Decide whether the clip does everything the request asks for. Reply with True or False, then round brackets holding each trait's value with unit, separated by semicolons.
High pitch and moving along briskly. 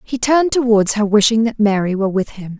True (220 Hz; 230 wpm)